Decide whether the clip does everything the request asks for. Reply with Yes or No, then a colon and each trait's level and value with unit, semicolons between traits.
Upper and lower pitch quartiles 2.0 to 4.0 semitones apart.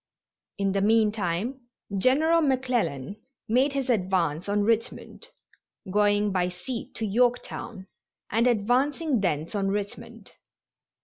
No: average, 4.4 semitones